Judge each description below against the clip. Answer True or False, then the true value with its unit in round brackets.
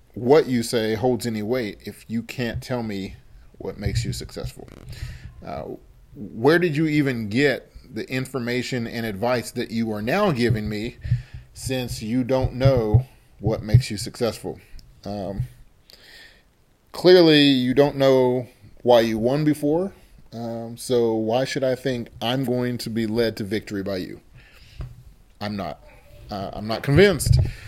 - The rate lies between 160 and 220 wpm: False (150 wpm)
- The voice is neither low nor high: False (120 Hz)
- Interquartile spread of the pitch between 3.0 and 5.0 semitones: False (2.6 semitones)